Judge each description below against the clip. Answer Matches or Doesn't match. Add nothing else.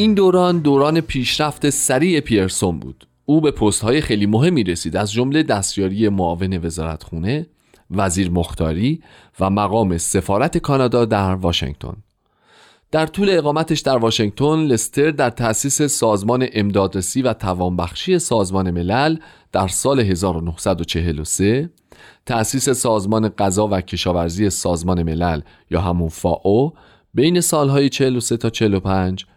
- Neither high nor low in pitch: Doesn't match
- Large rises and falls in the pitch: Matches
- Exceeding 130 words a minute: Doesn't match